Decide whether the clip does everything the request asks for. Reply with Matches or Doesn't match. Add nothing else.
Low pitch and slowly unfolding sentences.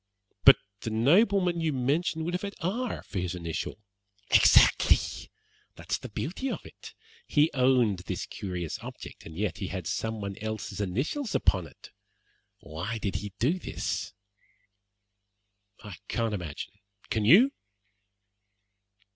Matches